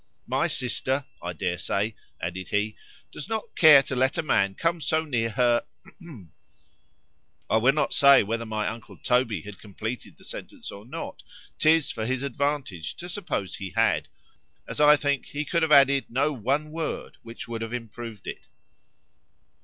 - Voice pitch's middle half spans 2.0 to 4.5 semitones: No, average, 5.1 semitones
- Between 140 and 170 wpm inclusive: Yes, average, 160 wpm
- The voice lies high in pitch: No, low, 125 Hz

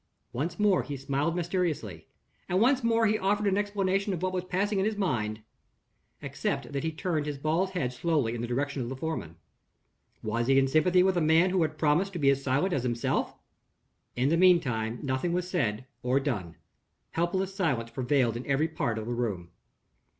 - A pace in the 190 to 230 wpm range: Yes, average, 195 wpm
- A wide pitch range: Yes, wide, 6.6 semitones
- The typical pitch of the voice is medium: Yes, medium, 155 Hz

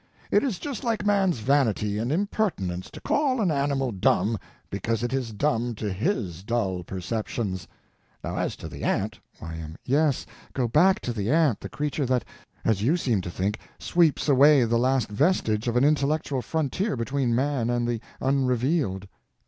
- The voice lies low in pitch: Yes, low, 125 Hz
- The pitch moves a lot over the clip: Yes, wide, 5.7 semitones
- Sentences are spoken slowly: No, average, 165 wpm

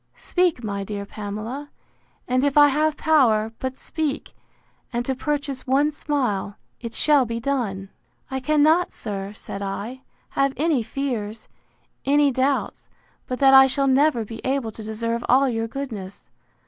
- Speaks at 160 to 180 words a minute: No, average, 150 wpm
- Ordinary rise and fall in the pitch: Yes, average, 4.3 semitones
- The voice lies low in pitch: No, very high, 260 Hz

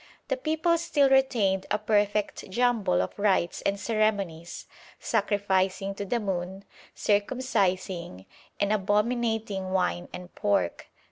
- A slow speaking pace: Yes, slow, 115 wpm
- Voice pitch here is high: Yes, high, 205 Hz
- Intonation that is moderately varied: Yes, average, 3.0 semitones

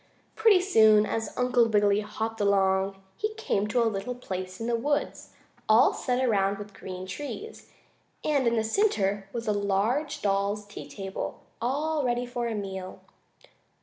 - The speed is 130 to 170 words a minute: Yes, average, 160 wpm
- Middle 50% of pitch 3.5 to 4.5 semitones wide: Yes, average, 3.9 semitones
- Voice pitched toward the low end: No, high, 220 Hz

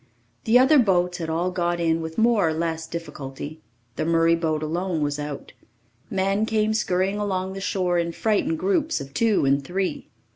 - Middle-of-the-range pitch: Yes, medium, 175 Hz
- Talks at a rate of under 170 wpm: No, average, 180 wpm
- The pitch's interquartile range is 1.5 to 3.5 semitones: No, average, 4.1 semitones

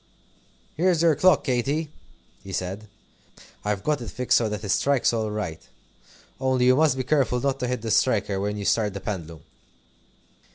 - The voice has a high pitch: No, low, 120 Hz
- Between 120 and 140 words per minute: No, average, 175 wpm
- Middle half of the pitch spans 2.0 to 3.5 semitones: No, average, 4.9 semitones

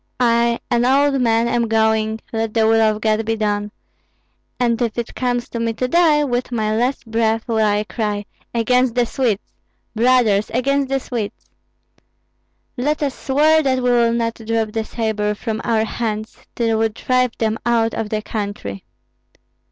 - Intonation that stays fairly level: Yes, narrow, 2.2 semitones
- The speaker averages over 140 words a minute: Yes, average, 170 wpm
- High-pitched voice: Yes, high, 230 Hz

